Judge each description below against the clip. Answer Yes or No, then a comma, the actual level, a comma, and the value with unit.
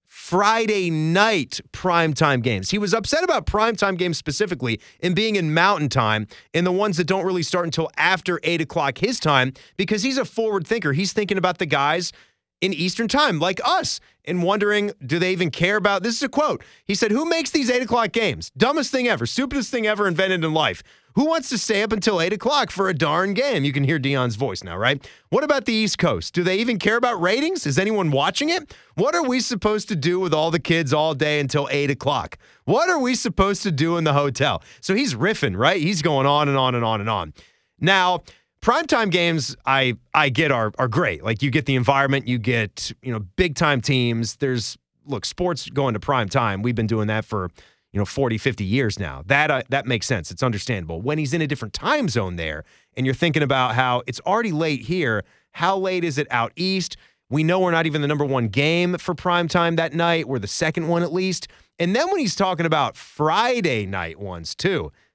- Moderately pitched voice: Yes, medium, 165 Hz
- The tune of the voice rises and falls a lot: Yes, wide, 6.8 semitones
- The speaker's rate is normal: No, fast, 220 wpm